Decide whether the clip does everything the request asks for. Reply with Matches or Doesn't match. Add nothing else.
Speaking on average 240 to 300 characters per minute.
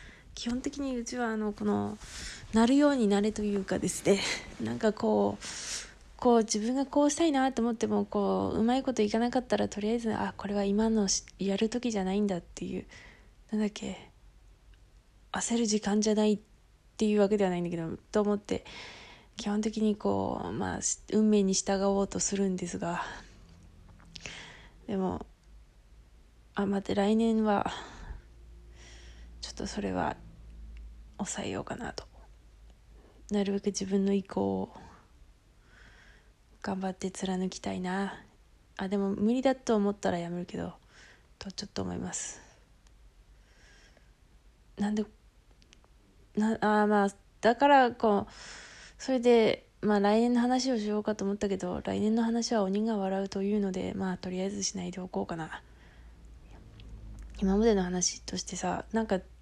Matches